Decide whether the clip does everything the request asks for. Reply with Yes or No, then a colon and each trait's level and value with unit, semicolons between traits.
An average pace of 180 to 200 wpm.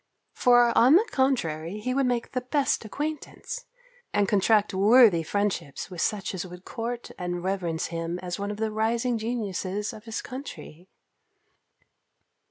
No: average, 150 wpm